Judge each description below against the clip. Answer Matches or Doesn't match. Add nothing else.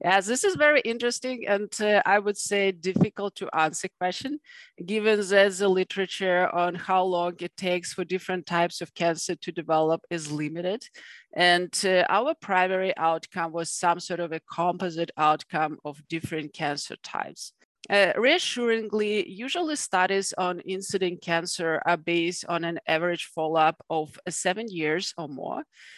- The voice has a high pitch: Doesn't match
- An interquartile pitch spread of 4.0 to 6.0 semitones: Doesn't match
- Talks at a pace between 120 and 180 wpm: Matches